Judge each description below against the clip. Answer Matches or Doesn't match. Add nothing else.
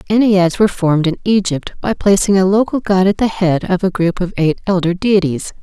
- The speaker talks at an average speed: Doesn't match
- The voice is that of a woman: Matches